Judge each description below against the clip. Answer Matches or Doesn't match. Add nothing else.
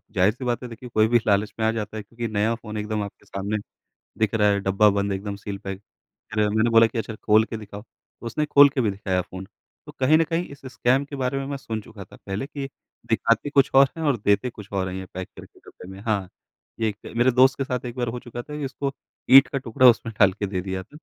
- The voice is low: Matches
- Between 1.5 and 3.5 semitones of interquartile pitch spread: Doesn't match